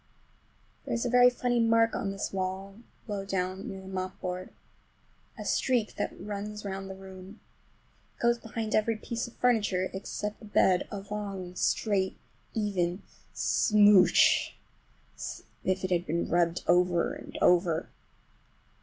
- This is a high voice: Yes, high, 195 Hz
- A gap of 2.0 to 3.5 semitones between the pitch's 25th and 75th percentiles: Yes, narrow, 2.6 semitones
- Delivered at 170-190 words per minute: No, average, 145 wpm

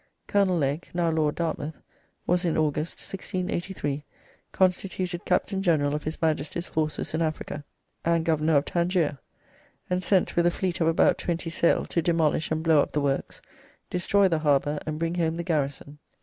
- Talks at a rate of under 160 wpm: No, average, 170 wpm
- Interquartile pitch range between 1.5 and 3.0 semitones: Yes, narrow, 2.5 semitones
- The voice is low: No, medium, 165 Hz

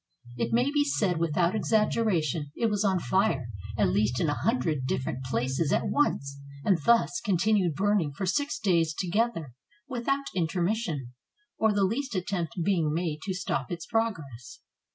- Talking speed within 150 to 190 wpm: Yes, average, 155 wpm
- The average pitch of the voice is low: No, medium, 180 Hz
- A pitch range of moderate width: No, wide, 6.4 semitones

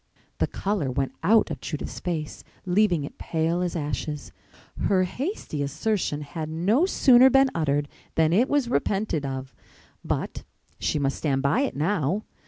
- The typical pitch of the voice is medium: Yes, medium, 165 Hz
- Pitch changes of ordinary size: No, wide, 6.5 semitones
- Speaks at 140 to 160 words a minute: Yes, average, 155 wpm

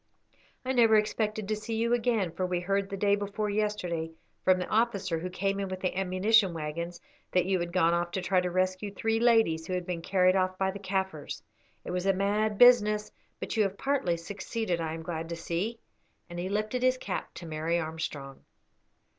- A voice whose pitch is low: No, high, 190 Hz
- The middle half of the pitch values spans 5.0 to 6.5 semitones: No, average, 3.5 semitones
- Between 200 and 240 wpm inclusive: Yes, fast, 205 wpm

